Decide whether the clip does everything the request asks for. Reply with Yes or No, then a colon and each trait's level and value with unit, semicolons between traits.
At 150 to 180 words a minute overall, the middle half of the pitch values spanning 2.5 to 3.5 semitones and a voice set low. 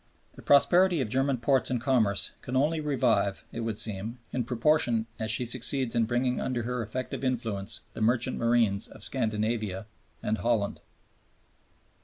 Yes: average, 160 wpm; average, 2.8 semitones; low, 120 Hz